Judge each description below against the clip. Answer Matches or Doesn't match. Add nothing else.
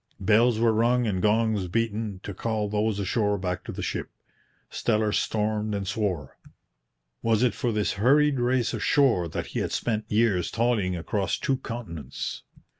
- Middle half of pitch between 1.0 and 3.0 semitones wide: Matches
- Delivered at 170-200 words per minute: Doesn't match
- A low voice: Matches